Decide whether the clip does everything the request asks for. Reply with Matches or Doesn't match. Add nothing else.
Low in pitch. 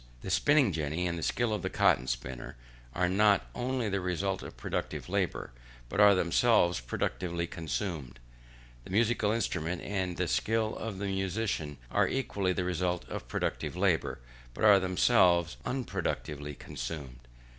Matches